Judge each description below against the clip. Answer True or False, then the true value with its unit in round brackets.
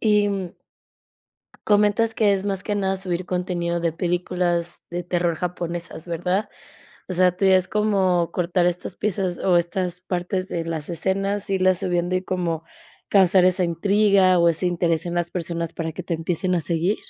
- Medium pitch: True (180 Hz)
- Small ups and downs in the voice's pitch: True (1.9 semitones)